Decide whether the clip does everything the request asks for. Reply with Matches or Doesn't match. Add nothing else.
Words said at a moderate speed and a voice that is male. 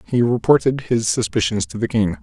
Matches